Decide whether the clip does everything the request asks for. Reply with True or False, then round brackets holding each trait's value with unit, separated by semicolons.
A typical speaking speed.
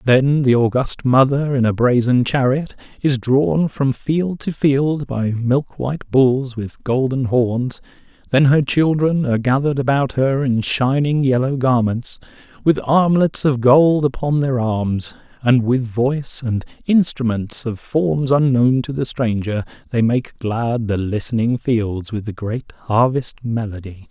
True (150 wpm)